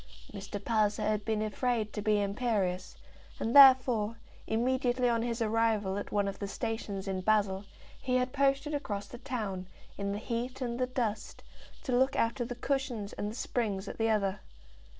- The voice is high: Yes, high, 225 Hz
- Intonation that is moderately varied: Yes, average, 3.4 semitones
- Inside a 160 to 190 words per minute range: Yes, average, 175 wpm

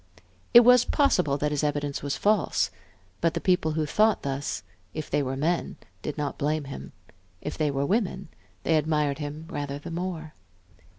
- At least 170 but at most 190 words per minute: Yes, average, 175 wpm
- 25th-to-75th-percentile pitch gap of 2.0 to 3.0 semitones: No, average, 3.4 semitones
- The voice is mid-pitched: Yes, medium, 150 Hz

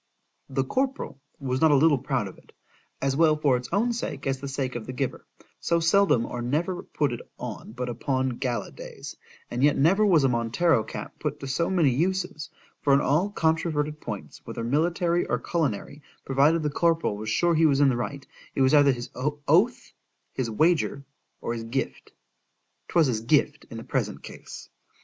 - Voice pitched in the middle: Yes, medium, 145 Hz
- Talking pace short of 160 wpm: No, average, 185 wpm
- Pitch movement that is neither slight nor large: Yes, average, 4.4 semitones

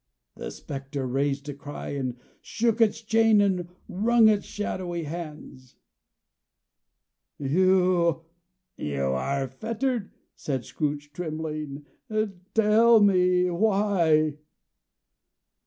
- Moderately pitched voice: Yes, medium, 170 Hz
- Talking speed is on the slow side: Yes, slow, 90 wpm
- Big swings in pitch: Yes, wide, 6.3 semitones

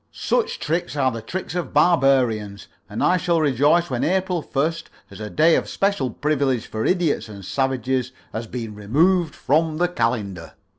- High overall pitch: No, medium, 140 Hz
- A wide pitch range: Yes, wide, 6.4 semitones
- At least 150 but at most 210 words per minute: Yes, average, 165 wpm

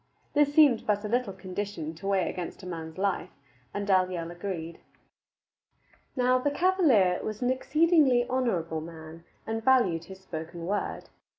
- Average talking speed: Yes, average, 150 wpm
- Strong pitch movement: Yes, wide, 6.7 semitones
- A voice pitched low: No, high, 200 Hz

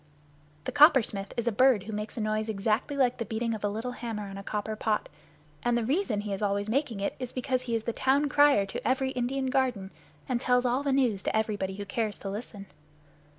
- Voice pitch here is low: No, high, 230 Hz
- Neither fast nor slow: No, fast, 230 wpm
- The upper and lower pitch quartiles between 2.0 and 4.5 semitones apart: Yes, average, 3.7 semitones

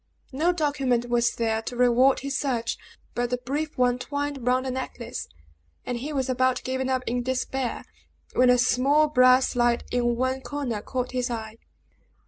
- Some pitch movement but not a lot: No, narrow, 1.7 semitones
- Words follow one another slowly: No, average, 170 wpm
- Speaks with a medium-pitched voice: No, very high, 255 Hz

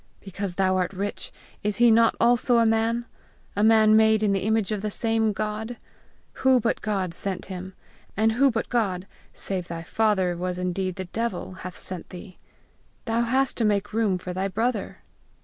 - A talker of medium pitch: No, high, 210 Hz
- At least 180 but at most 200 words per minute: Yes, average, 185 wpm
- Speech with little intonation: No, average, 3.2 semitones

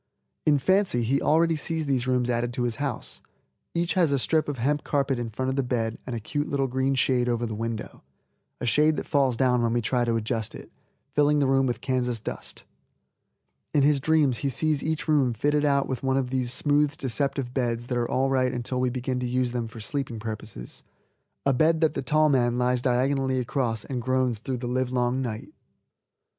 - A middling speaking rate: No, fast, 210 wpm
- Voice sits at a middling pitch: No, low, 130 Hz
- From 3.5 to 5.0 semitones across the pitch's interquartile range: No, narrow, 2.6 semitones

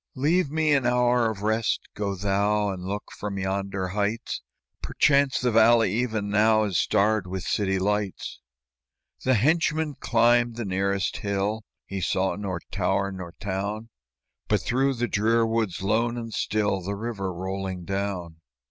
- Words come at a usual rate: Yes, average, 150 wpm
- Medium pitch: No, low, 105 Hz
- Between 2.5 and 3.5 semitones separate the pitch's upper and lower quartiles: Yes, average, 3.2 semitones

